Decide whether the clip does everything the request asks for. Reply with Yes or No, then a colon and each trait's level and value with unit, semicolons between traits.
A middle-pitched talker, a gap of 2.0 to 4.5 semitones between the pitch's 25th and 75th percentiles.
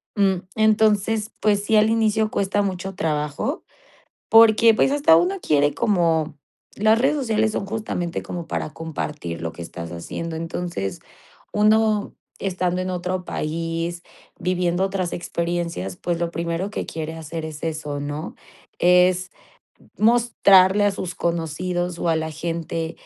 Yes: medium, 180 Hz; average, 4.1 semitones